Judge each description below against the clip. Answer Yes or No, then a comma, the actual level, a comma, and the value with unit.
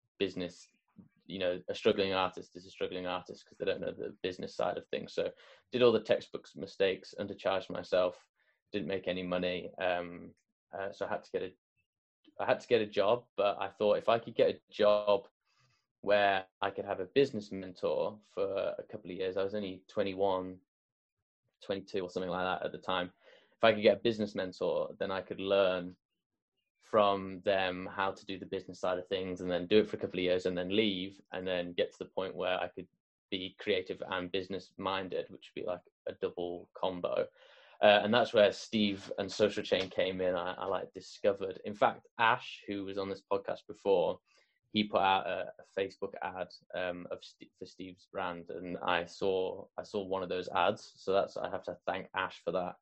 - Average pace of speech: No, fast, 210 wpm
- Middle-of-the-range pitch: No, low, 100 Hz